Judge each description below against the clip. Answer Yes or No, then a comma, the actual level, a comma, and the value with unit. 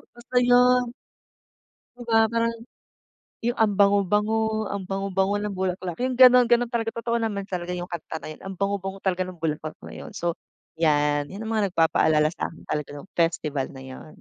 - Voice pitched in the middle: No, high, 195 Hz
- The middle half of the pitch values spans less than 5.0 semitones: No, average, 5.3 semitones